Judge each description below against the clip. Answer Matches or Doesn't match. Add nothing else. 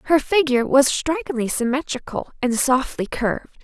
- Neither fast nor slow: Doesn't match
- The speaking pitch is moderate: Doesn't match